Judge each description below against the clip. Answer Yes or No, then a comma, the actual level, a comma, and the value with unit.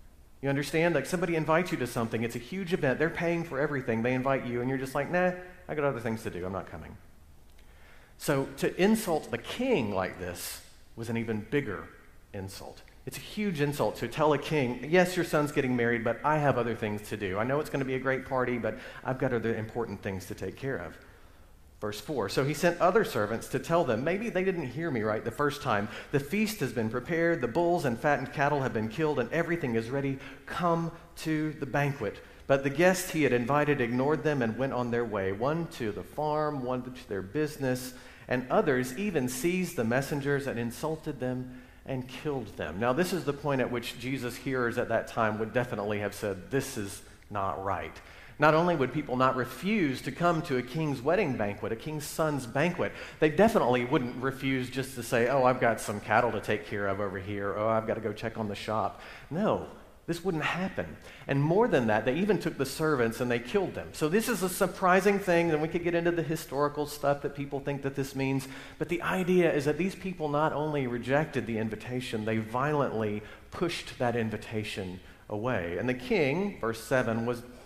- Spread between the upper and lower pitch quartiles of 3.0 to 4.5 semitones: No, average, 5.3 semitones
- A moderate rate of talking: No, fast, 220 wpm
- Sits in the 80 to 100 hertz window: No, low, 130 Hz